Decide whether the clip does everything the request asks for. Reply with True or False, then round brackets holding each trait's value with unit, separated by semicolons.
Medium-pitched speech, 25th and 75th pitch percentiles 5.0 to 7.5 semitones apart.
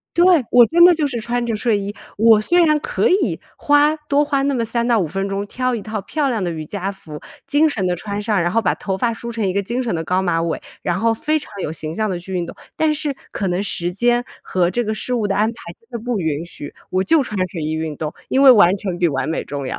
False (215 Hz; 5.4 semitones)